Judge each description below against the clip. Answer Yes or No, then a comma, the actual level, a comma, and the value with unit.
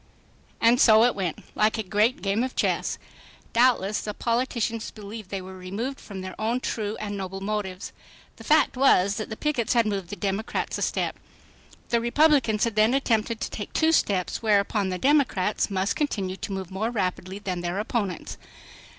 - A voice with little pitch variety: No, average, 3.4 semitones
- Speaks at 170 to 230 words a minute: Yes, average, 175 wpm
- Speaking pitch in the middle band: No, high, 210 Hz